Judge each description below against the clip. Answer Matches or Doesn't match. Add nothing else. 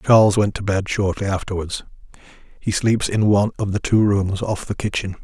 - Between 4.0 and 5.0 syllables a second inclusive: Doesn't match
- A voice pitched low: Matches